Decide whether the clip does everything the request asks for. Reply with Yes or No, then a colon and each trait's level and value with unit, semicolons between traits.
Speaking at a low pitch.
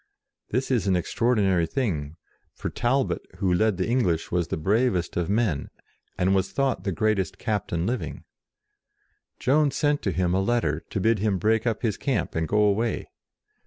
Yes: low, 105 Hz